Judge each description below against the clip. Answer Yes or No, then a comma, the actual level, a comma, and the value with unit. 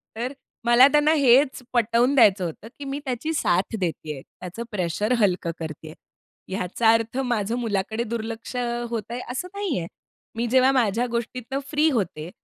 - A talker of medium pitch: No, high, 230 Hz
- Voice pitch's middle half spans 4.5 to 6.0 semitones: Yes, average, 4.8 semitones